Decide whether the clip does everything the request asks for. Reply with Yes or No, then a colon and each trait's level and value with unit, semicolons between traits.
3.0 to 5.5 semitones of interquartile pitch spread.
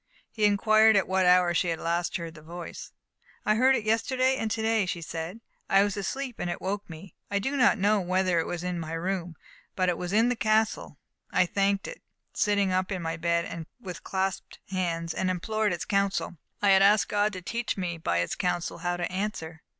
Yes: average, 3.5 semitones